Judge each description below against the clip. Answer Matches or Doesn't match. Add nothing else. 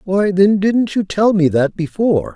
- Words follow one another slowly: Doesn't match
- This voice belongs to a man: Matches